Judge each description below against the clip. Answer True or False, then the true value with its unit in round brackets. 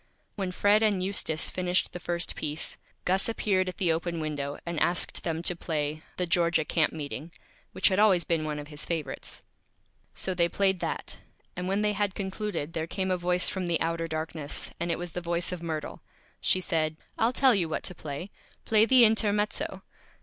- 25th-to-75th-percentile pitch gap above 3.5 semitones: False (3.1 semitones)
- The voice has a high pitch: False (175 Hz)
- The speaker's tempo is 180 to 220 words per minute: True (195 wpm)